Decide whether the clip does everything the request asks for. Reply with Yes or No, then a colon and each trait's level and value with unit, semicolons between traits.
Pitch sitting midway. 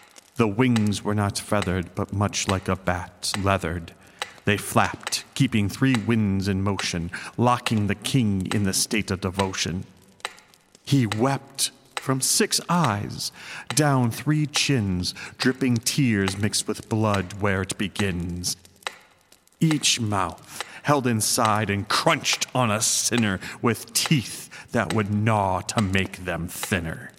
No: low, 105 Hz